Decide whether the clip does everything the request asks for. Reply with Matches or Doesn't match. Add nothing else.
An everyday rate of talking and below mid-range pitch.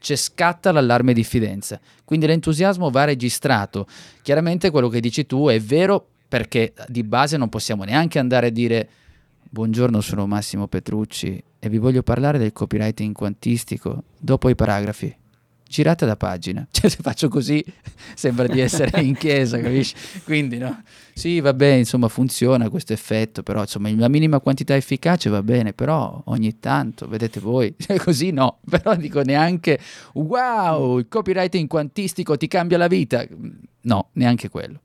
Matches